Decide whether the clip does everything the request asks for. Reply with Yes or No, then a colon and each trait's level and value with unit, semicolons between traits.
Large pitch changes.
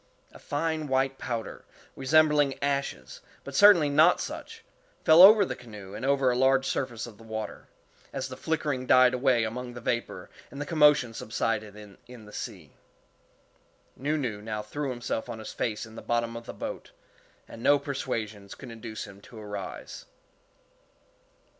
No: average, 4.3 semitones